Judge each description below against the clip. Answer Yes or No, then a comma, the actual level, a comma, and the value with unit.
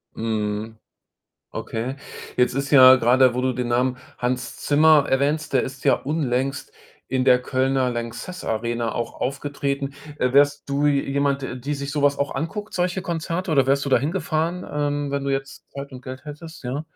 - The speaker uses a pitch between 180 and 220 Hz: No, low, 135 Hz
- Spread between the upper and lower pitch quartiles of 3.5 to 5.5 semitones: No, narrow, 2.4 semitones